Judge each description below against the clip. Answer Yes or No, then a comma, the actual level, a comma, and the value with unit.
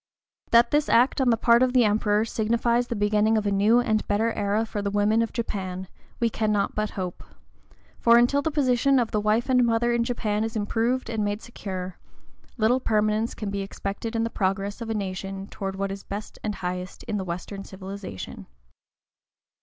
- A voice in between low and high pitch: No, high, 215 Hz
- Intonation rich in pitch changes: No, average, 2.8 semitones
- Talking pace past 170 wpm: Yes, average, 195 wpm